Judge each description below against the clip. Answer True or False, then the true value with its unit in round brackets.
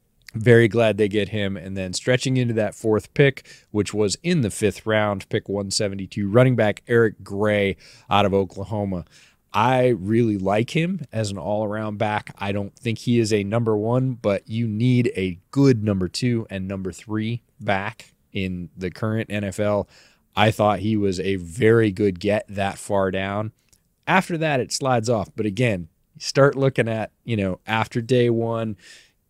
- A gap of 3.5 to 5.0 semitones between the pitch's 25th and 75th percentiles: False (3.1 semitones)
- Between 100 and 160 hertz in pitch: True (110 Hz)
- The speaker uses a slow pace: False (175 wpm)